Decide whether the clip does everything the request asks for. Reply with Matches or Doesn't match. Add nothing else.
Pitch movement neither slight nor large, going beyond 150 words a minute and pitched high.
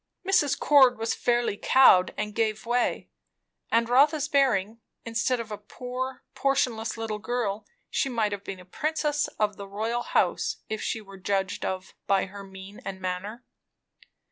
Matches